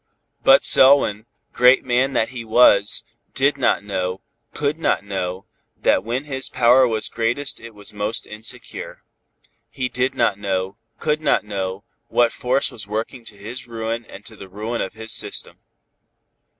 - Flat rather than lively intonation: No, average, 4.0 semitones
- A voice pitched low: Yes, low, 115 Hz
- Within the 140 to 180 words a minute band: Yes, average, 160 wpm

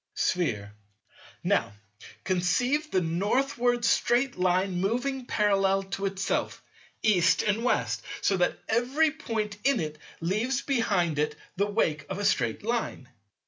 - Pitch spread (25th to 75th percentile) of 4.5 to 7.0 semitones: Yes, average, 5.2 semitones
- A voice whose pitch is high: Yes, high, 200 Hz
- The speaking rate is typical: No, slow, 130 wpm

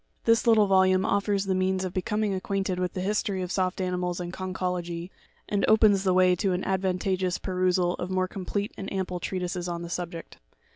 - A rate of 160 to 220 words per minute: Yes, average, 190 wpm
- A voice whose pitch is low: No, medium, 185 Hz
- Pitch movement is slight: Yes, narrow, 1.4 semitones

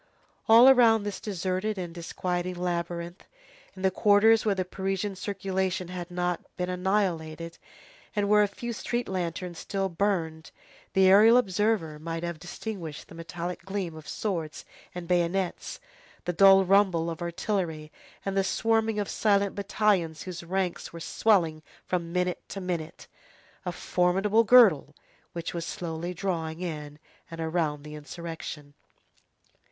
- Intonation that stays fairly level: No, average, 3.0 semitones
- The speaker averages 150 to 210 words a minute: No, average, 140 wpm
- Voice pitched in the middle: Yes, medium, 180 Hz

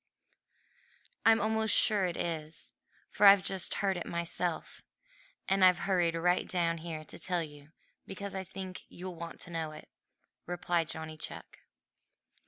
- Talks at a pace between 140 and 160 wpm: Yes, average, 150 wpm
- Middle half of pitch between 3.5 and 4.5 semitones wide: No, narrow, 2.4 semitones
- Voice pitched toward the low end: No, medium, 175 Hz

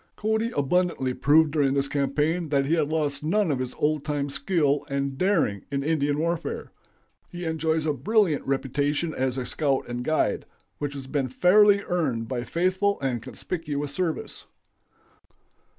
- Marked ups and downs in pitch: No, average, 3.4 semitones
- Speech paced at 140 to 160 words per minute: Yes, average, 155 wpm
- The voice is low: No, medium, 145 Hz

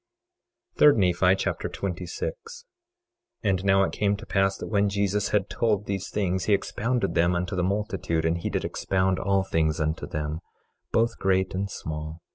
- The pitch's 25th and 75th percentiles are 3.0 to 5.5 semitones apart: No, narrow, 2.6 semitones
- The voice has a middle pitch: No, very low, 95 Hz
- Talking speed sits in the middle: Yes, average, 175 wpm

